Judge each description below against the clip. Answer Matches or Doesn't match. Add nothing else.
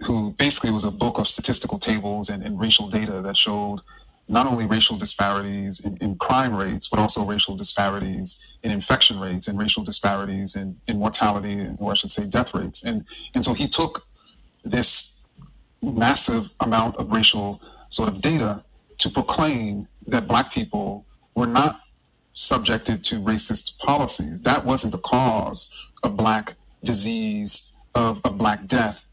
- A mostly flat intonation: Matches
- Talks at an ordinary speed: Matches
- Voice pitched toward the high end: Doesn't match